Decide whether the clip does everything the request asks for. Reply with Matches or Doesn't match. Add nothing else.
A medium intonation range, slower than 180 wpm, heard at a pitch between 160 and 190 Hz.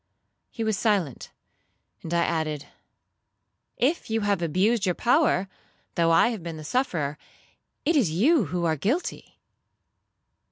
Doesn't match